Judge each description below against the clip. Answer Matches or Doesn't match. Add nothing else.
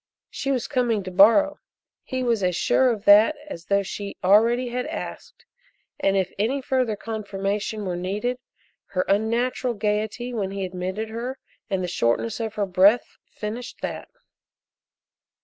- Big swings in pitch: Doesn't match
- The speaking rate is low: Doesn't match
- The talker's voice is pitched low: Doesn't match